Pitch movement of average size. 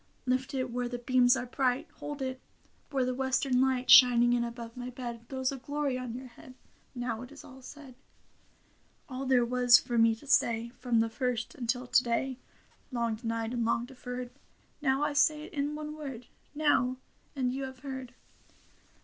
No: narrow, 1.6 semitones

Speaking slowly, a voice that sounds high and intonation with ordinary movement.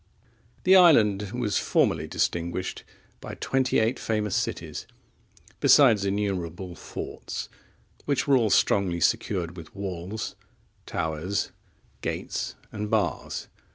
No: slow, 105 wpm; low, 100 Hz; average, 4.1 semitones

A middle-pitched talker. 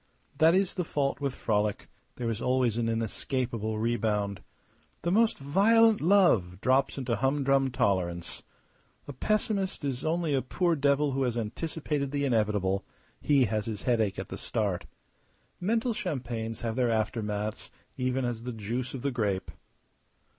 No: low, 125 Hz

